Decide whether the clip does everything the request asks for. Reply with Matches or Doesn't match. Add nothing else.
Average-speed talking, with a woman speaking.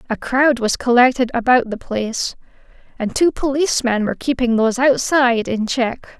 Matches